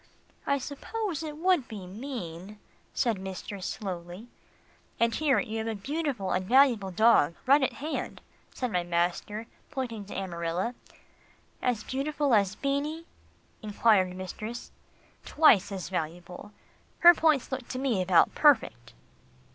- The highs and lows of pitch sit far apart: Yes, wide, 6.7 semitones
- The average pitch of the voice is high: Yes, high, 220 Hz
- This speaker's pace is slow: Yes, slow, 130 wpm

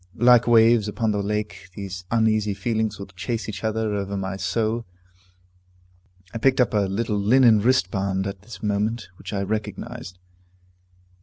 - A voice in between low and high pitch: No, low, 105 Hz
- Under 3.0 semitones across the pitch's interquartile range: Yes, narrow, 2.4 semitones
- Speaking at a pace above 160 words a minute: No, average, 150 wpm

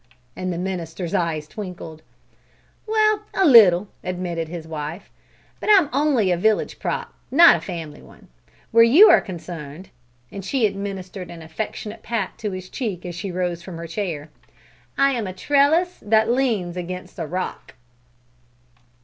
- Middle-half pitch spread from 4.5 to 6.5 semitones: Yes, average, 5.0 semitones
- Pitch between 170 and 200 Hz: Yes, medium, 185 Hz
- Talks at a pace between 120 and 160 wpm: Yes, average, 150 wpm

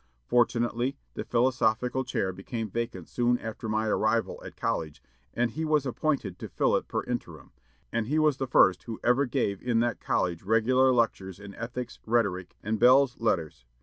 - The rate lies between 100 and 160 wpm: No, average, 175 wpm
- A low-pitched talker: Yes, low, 115 Hz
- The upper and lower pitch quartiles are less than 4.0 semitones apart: Yes, average, 3.0 semitones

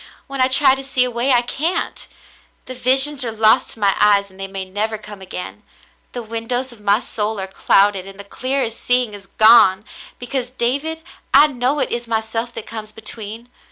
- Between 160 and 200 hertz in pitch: No, high, 230 Hz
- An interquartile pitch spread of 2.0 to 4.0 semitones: Yes, average, 3.6 semitones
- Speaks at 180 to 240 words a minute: Yes, average, 195 wpm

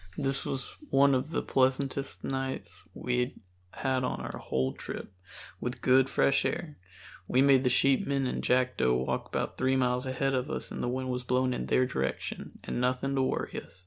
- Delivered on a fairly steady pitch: Yes, narrow, 1.4 semitones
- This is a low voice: Yes, low, 130 Hz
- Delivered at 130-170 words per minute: No, average, 185 wpm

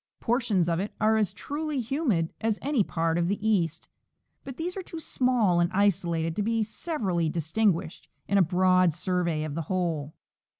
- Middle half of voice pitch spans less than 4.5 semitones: No, average, 5.2 semitones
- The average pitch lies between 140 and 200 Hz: Yes, high, 190 Hz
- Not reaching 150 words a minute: No, average, 175 wpm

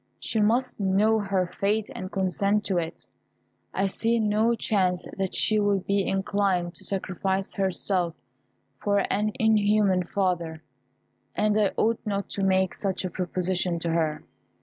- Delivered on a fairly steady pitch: Yes, narrow, 2.2 semitones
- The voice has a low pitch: No, high, 195 Hz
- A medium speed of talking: Yes, average, 150 wpm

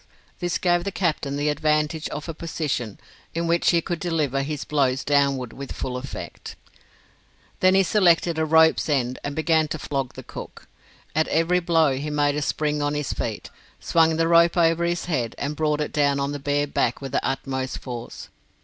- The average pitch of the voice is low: No, medium, 150 Hz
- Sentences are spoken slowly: No, average, 195 wpm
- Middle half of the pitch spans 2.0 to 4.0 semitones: Yes, average, 3.0 semitones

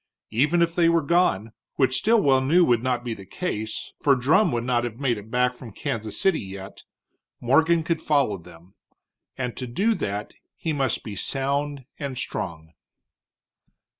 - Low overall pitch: Yes, low, 130 Hz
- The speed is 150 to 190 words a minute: Yes, average, 165 wpm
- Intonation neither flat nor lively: No, wide, 5.8 semitones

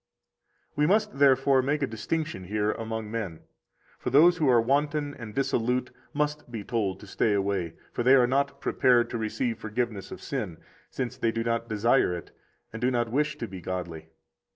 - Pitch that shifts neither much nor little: Yes, average, 4.4 semitones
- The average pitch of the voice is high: No, low, 120 Hz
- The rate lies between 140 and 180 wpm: No, average, 190 wpm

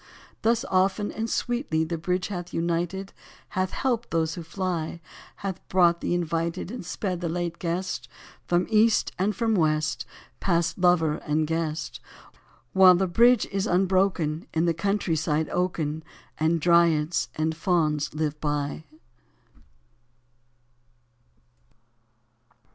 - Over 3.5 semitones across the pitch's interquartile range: No, average, 3.0 semitones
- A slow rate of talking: Yes, slow, 120 wpm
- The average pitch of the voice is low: No, medium, 175 Hz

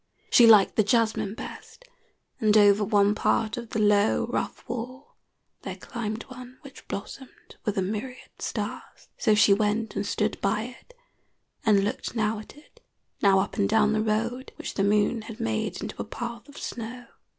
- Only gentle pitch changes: Yes, narrow, 2.3 semitones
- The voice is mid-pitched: No, high, 215 Hz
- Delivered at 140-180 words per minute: Yes, average, 175 wpm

